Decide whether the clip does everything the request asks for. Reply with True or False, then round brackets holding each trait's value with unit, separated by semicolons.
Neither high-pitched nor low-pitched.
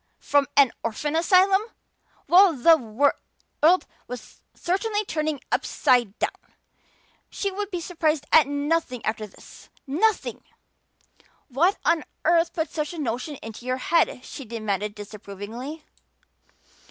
False (295 Hz)